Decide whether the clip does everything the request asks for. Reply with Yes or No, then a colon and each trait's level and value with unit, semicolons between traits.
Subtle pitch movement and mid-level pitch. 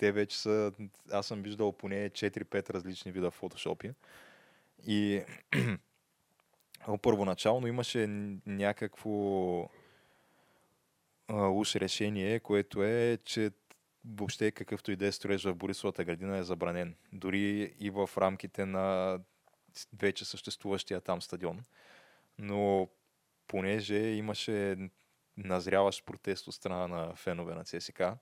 No: narrow, 1.6 semitones; low, 100 Hz